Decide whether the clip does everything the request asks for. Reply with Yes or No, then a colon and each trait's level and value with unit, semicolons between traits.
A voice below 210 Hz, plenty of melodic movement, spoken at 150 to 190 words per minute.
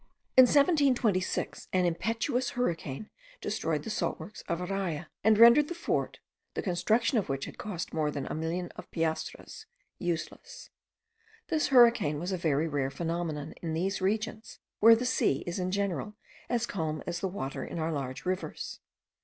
Yes: medium, 185 Hz; wide, 5.8 semitones; average, 165 wpm